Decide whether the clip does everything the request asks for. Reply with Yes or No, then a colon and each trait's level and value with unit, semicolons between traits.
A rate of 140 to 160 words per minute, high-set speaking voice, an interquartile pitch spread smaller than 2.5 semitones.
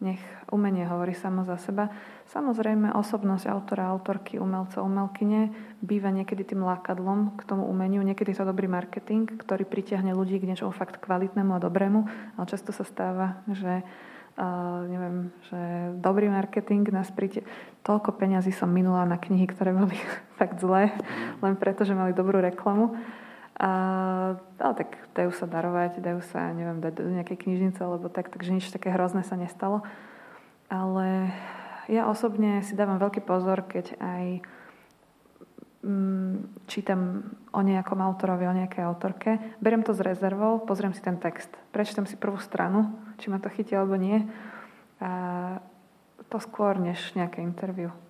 Yes: average, 150 wpm; high, 195 Hz; narrow, 2.1 semitones